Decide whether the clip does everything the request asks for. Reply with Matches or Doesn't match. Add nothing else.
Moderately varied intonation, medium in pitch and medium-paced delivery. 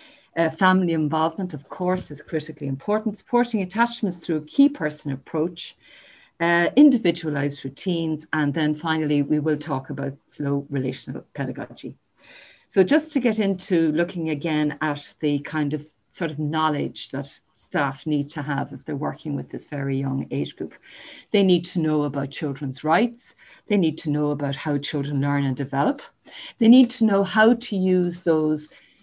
Matches